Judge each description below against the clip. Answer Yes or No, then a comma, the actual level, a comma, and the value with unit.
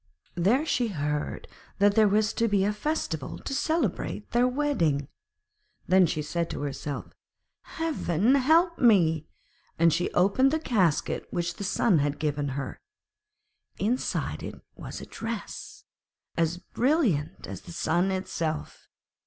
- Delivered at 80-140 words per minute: Yes, slow, 135 wpm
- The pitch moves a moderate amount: No, wide, 7.3 semitones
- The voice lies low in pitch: No, high, 190 Hz